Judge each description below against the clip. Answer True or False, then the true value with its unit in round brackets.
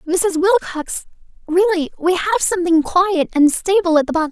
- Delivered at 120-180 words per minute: True (140 wpm)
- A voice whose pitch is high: True (350 Hz)